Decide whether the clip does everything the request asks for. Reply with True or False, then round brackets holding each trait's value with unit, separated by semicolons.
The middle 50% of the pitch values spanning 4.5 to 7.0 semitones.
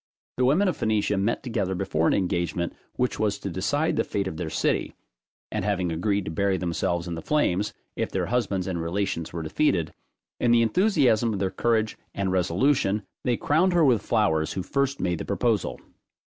True (5.2 semitones)